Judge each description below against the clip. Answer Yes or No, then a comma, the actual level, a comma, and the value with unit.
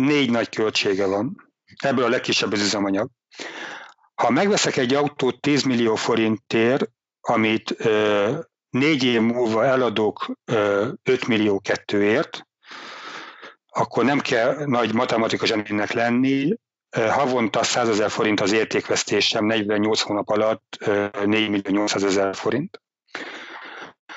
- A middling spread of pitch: Yes, average, 3.9 semitones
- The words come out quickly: No, average, 120 wpm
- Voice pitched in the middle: No, low, 115 Hz